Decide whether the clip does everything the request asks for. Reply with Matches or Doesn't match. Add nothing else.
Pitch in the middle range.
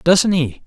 Matches